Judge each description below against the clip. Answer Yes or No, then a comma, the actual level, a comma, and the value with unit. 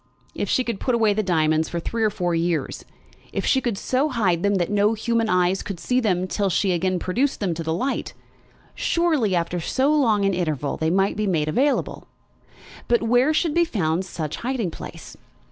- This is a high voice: Yes, high, 200 Hz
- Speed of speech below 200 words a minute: No, fast, 205 wpm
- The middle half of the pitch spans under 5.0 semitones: No, wide, 5.5 semitones